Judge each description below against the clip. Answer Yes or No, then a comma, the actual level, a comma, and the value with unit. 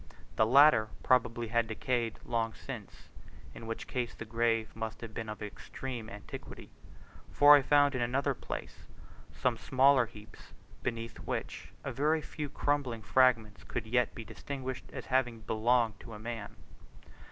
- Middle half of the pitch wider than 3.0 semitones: No, average, 2.7 semitones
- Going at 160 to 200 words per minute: No, average, 150 wpm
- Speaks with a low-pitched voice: Yes, low, 120 Hz